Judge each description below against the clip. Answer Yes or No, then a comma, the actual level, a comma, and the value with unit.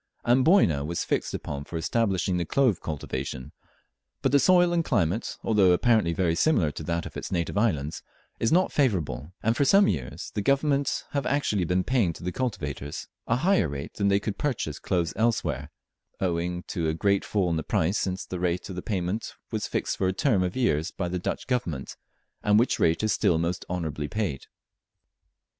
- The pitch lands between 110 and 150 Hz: No, very low, 90 Hz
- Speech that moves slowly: No, average, 190 wpm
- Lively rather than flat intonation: Yes, wide, 5.8 semitones